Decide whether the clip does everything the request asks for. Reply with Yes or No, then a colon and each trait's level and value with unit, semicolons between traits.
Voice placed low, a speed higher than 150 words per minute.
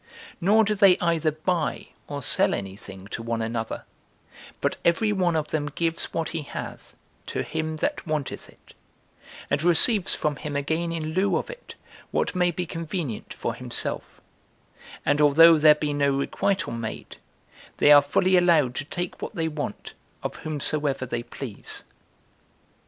No: medium, 155 Hz; average, 160 wpm